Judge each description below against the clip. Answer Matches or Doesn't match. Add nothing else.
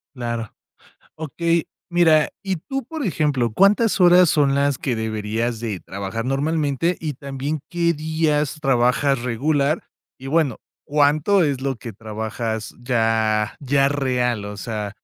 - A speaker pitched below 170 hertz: Matches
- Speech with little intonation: Doesn't match